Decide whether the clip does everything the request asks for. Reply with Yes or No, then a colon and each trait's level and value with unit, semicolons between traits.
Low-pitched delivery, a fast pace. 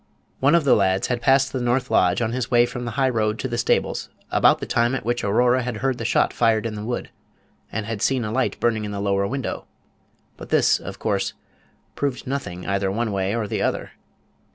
Yes: low, 120 Hz; fast, 225 wpm